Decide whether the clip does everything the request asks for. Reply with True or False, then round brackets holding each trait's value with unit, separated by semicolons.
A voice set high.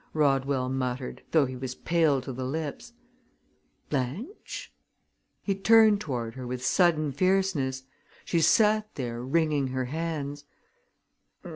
False (145 Hz)